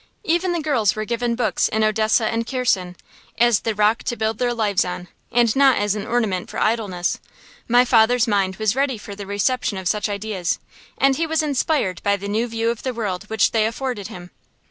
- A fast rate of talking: Yes, fast, 210 wpm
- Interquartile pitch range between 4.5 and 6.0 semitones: No, average, 3.2 semitones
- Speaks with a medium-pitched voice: No, high, 220 Hz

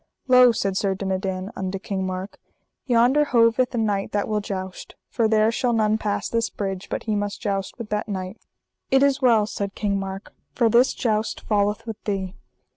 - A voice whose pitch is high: Yes, high, 210 Hz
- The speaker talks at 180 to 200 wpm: Yes, average, 190 wpm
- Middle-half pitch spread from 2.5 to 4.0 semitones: Yes, average, 2.9 semitones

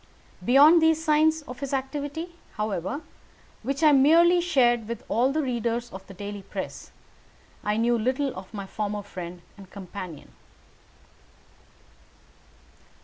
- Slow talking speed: Yes, slow, 130 wpm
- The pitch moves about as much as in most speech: No, wide, 6.4 semitones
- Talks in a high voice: Yes, high, 240 Hz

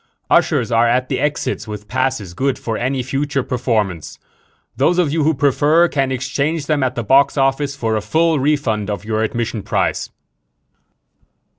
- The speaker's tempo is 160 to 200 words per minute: Yes, average, 165 wpm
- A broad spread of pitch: No, average, 4.3 semitones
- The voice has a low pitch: Yes, low, 130 Hz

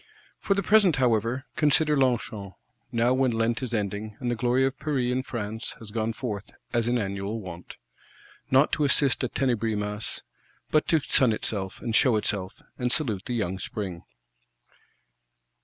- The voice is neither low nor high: No, low, 115 Hz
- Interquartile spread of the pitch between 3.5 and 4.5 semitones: Yes, average, 3.9 semitones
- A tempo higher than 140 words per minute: Yes, average, 165 wpm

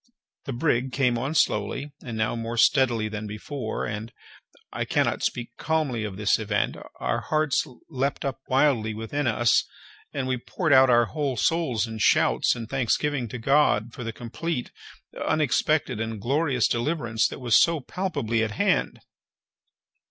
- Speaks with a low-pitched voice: Yes, low, 125 Hz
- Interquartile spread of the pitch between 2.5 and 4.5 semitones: Yes, average, 4.2 semitones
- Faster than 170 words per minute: No, average, 150 wpm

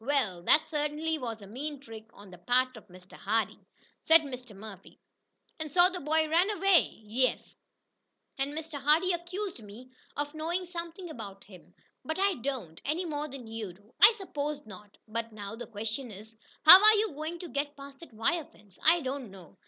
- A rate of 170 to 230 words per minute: Yes, average, 190 wpm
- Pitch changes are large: Yes, wide, 6.6 semitones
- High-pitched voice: Yes, very high, 280 Hz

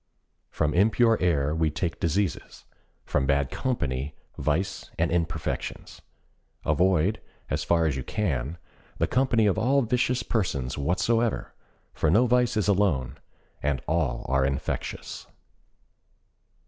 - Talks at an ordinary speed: No, slow, 120 wpm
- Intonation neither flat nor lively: No, wide, 7.3 semitones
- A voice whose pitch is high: No, very low, 85 Hz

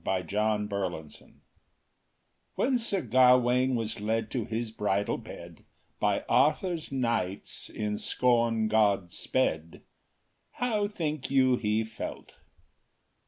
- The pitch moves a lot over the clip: No, average, 3.7 semitones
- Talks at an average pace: No, slow, 120 wpm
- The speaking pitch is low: Yes, low, 115 Hz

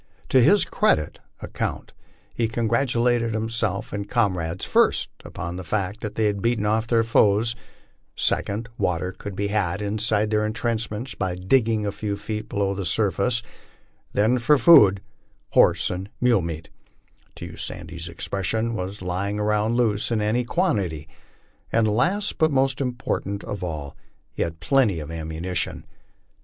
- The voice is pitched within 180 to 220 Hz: No, low, 105 Hz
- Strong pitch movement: No, average, 3.7 semitones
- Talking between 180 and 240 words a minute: No, average, 155 wpm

